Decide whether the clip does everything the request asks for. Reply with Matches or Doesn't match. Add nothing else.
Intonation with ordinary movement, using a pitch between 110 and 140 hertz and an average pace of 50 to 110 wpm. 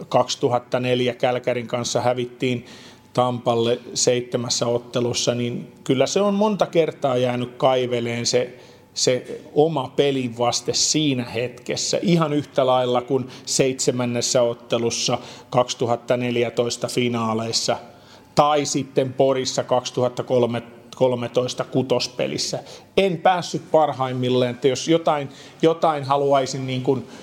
Doesn't match